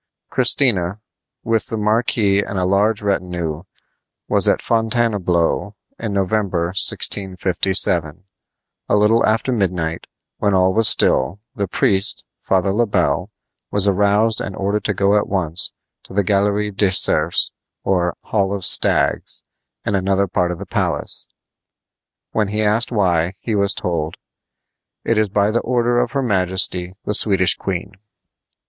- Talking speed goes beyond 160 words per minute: No, average, 140 wpm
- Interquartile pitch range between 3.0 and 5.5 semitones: No, narrow, 2.6 semitones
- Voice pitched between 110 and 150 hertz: No, low, 100 Hz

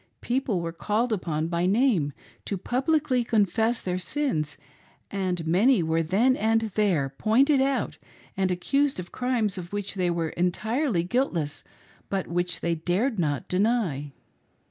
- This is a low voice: No, high, 195 Hz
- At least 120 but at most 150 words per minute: Yes, average, 145 wpm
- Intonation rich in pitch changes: Yes, wide, 6.0 semitones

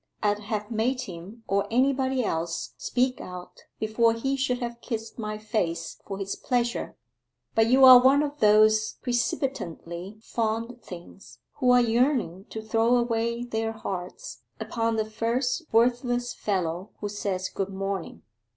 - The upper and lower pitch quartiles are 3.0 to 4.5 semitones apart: Yes, average, 3.5 semitones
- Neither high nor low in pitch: No, high, 225 Hz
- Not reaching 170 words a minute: Yes, average, 145 wpm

